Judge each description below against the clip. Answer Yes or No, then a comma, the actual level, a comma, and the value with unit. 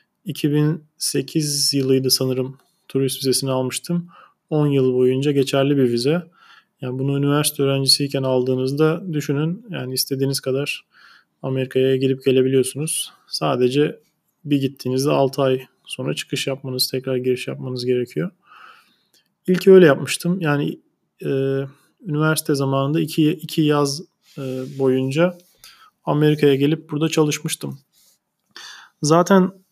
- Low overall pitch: No, medium, 145 Hz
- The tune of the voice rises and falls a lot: No, average, 3.4 semitones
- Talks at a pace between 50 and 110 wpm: Yes, average, 105 wpm